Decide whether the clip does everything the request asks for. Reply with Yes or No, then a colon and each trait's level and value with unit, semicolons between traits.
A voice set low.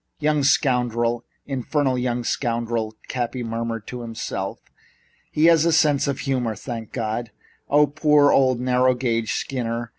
Yes: low, 125 Hz